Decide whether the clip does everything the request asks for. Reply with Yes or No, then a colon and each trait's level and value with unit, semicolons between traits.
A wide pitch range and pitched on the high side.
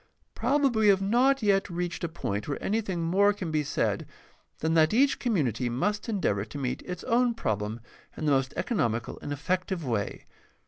No: wide, 7.9 semitones; medium, 175 Hz